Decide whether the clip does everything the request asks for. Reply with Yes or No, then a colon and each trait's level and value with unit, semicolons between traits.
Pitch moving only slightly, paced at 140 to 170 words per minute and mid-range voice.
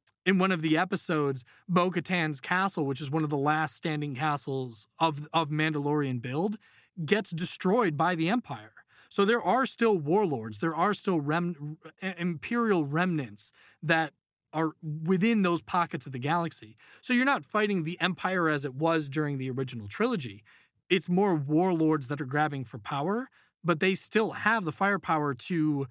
No: average, 4.0 semitones; average, 165 wpm; medium, 165 Hz